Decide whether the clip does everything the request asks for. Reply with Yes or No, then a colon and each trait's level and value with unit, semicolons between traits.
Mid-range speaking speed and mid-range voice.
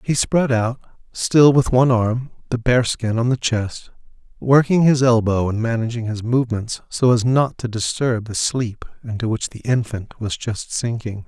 No: average, 180 wpm; low, 120 Hz